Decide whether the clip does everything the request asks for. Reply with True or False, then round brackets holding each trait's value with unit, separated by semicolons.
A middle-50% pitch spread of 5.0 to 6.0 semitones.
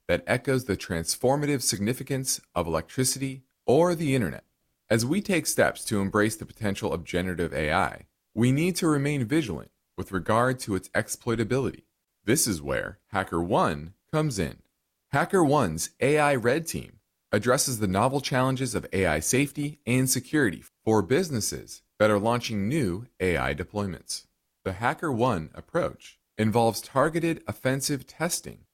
True (5.4 semitones)